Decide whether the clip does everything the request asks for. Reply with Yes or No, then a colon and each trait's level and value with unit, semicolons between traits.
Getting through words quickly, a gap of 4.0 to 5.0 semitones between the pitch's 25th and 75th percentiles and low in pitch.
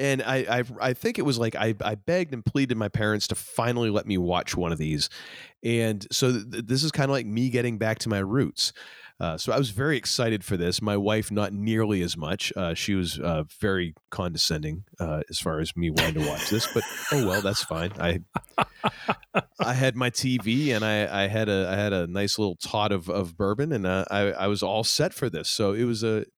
Yes: fast, 235 wpm; average, 4.7 semitones; low, 105 Hz